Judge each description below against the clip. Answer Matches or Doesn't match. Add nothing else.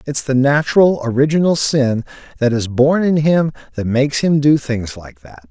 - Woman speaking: Doesn't match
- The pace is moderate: Matches